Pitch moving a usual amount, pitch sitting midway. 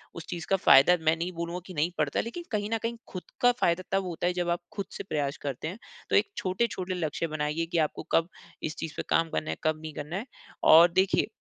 Yes: average, 3.0 semitones; medium, 170 Hz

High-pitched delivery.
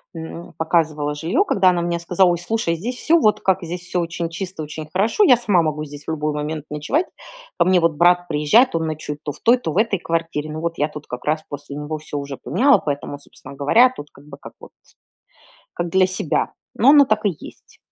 No: medium, 165 Hz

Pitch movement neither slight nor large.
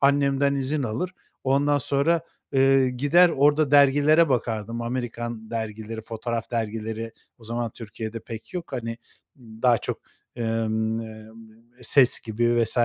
Yes: average, 3.7 semitones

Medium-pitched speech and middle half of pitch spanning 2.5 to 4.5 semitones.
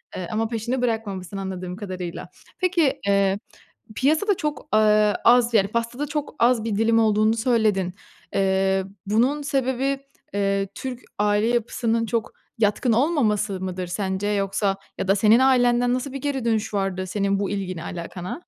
No: high, 215 Hz; average, 3.9 semitones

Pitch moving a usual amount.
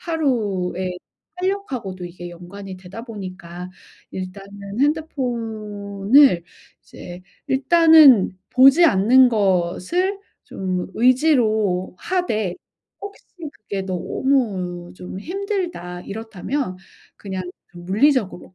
No: wide, 6.7 semitones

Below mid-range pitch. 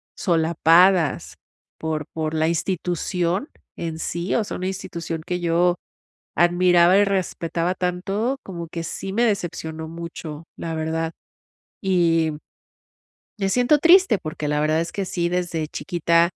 No: medium, 170 Hz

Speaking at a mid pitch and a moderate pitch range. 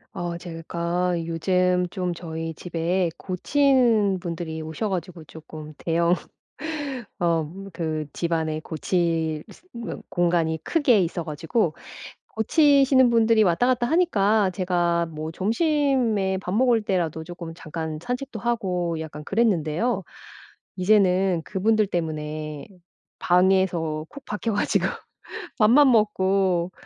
Yes: medium, 180 Hz; average, 4.8 semitones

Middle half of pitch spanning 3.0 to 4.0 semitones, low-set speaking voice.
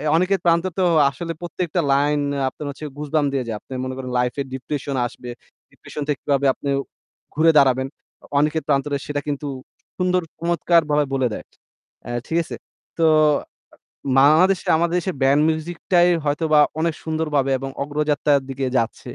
No: average, 3.3 semitones; medium, 150 Hz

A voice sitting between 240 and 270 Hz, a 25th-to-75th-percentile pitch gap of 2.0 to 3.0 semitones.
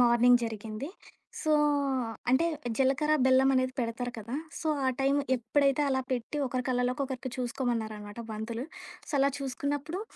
Yes: very high, 255 Hz; narrow, 2.5 semitones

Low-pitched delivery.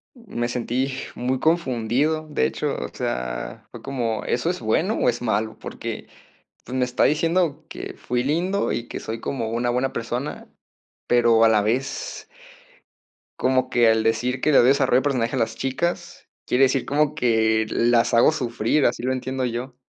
Yes: low, 125 Hz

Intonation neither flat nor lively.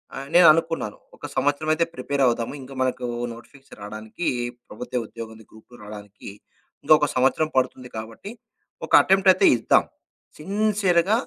No: wide, 6.4 semitones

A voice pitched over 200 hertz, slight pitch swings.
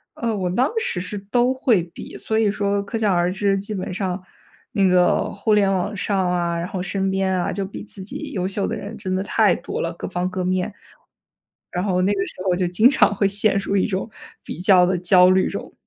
No: high, 195 Hz; narrow, 2.1 semitones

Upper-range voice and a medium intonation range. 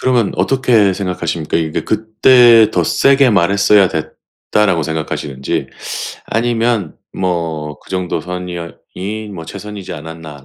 No: very low, 95 Hz; average, 5.0 semitones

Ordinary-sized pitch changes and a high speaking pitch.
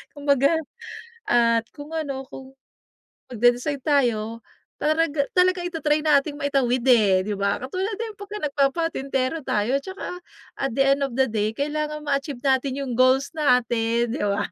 Yes: average, 3.8 semitones; very high, 275 Hz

